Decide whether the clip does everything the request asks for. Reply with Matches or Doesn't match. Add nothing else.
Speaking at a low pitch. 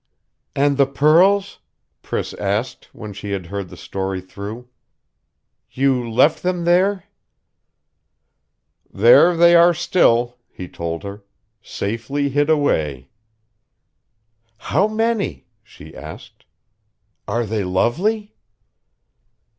Matches